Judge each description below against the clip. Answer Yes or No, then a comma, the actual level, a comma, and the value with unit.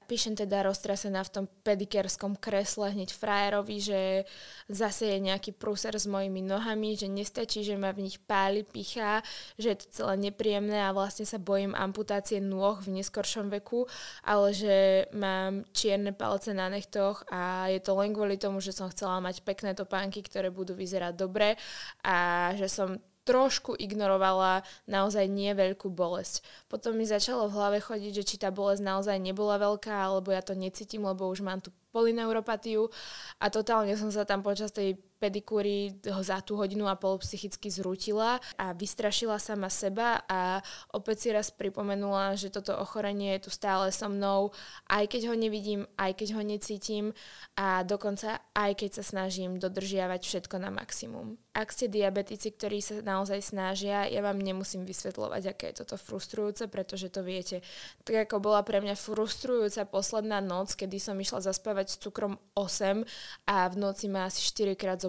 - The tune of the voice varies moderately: No, narrow, 1.6 semitones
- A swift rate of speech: Yes, fast, 170 wpm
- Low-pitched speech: No, high, 200 Hz